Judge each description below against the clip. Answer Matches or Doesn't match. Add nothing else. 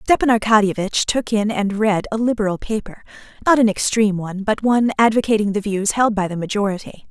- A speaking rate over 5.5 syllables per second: Matches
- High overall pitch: Matches